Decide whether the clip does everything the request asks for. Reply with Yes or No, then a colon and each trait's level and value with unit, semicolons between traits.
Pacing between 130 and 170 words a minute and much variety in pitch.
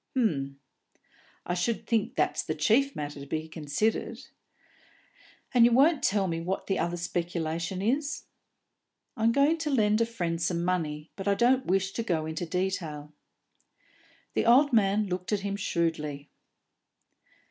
Yes: average, 150 wpm; wide, 5.7 semitones